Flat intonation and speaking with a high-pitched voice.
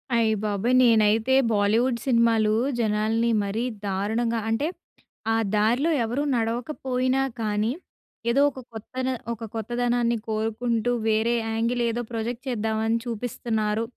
Yes: narrow, 1.8 semitones; high, 230 Hz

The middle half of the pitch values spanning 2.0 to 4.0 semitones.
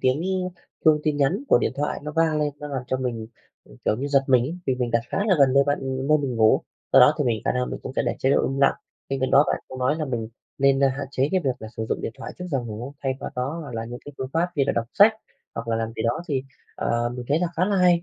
Yes: average, 3.3 semitones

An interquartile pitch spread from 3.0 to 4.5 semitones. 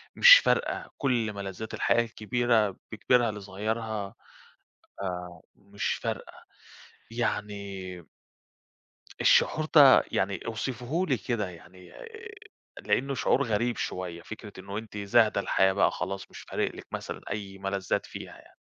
Yes: average, 3.4 semitones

